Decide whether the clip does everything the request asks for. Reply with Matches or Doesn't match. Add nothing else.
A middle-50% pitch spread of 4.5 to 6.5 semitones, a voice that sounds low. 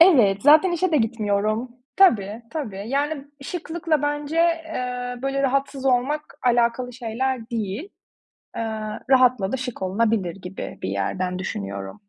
Doesn't match